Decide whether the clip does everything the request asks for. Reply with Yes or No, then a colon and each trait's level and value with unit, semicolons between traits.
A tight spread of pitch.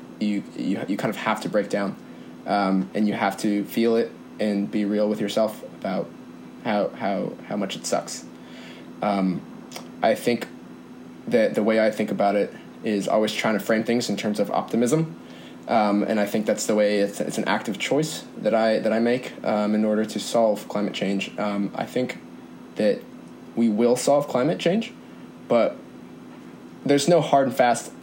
Yes: narrow, 1.8 semitones